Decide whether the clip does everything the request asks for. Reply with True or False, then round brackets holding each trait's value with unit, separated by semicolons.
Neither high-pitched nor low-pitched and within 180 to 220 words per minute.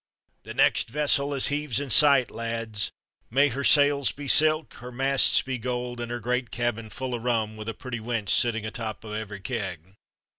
False (120 Hz; 190 wpm)